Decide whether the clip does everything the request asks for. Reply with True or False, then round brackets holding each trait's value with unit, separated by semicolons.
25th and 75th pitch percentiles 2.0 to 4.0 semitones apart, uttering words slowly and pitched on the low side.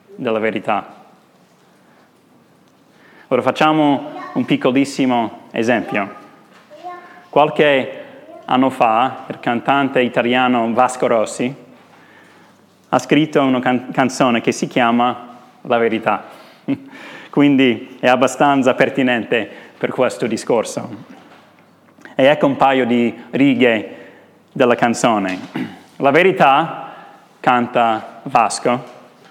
True (3.6 semitones; 90 wpm; 130 Hz)